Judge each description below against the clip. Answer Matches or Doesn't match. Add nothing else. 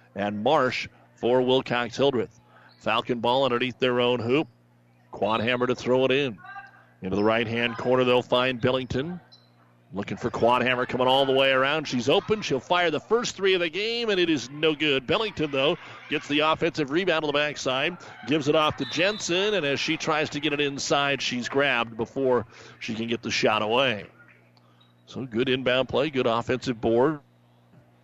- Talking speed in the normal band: Matches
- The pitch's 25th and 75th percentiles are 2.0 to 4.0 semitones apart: Doesn't match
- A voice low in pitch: Matches